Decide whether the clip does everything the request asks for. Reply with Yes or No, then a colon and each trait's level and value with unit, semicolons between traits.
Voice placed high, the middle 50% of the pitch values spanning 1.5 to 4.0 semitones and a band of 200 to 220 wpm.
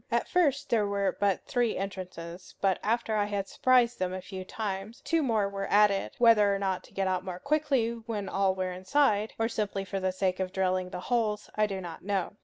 Yes: high, 200 Hz; average, 3.1 semitones; fast, 205 wpm